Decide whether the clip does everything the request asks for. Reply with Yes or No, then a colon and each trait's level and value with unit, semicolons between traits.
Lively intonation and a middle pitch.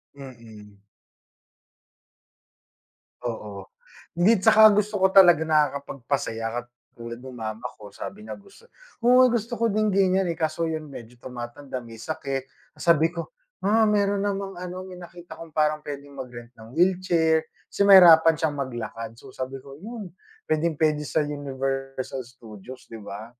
Yes: wide, 6.7 semitones; medium, 150 Hz